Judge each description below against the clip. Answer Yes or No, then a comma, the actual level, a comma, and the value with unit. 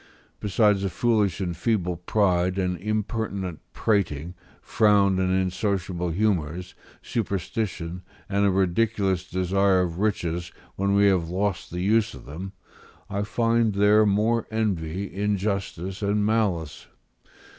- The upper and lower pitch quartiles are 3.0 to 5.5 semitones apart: No, narrow, 2.6 semitones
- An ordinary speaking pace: No, slow, 125 wpm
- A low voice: Yes, very low, 95 Hz